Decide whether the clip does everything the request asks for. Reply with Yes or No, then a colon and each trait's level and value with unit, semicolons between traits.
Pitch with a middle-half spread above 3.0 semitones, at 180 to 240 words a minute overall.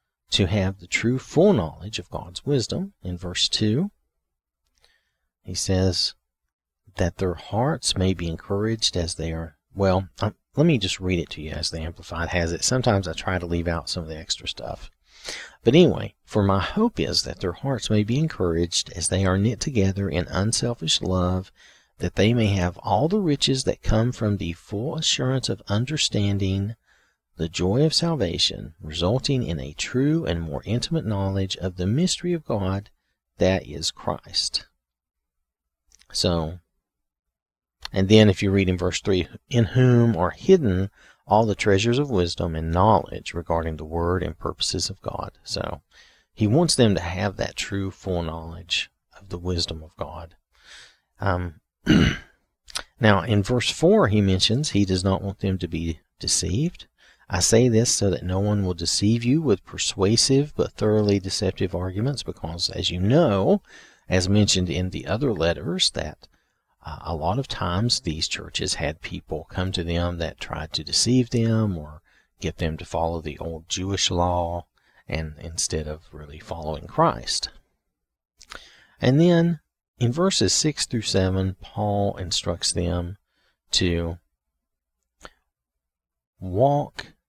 No: average, 4.5 semitones; average, 160 wpm